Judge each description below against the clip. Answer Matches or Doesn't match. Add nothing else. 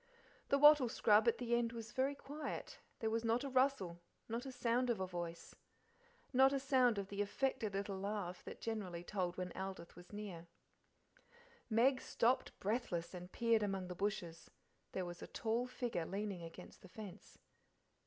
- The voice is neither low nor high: Doesn't match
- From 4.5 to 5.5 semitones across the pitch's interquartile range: Matches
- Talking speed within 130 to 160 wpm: Doesn't match